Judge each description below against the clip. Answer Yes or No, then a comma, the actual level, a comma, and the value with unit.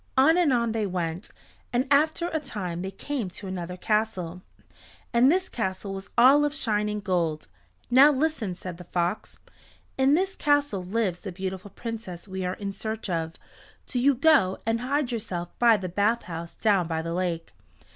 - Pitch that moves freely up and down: Yes, wide, 6.0 semitones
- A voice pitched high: Yes, high, 210 Hz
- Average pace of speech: Yes, average, 175 wpm